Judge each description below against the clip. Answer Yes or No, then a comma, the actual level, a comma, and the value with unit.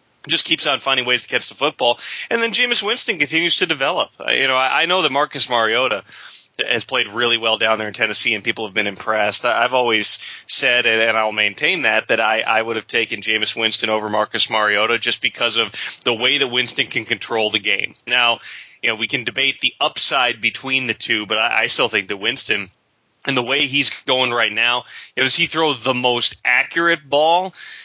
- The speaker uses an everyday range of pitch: Yes, average, 4.6 semitones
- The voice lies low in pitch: Yes, low, 125 Hz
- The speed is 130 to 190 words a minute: No, fast, 205 wpm